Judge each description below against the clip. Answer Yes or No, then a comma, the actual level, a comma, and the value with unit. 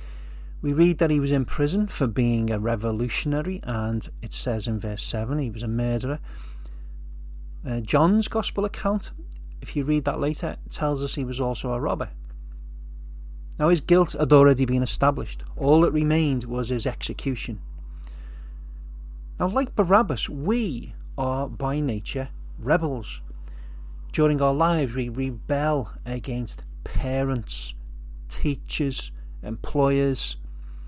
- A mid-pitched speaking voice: No, low, 125 Hz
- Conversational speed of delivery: No, slow, 130 wpm